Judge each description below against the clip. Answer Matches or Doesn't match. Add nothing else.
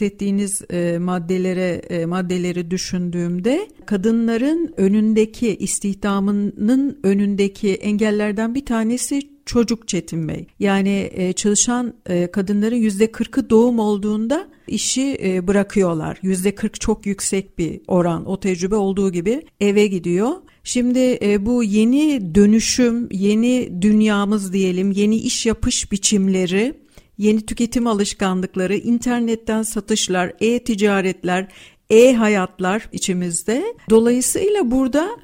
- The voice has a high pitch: Matches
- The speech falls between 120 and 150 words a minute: Doesn't match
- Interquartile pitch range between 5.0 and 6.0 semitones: Doesn't match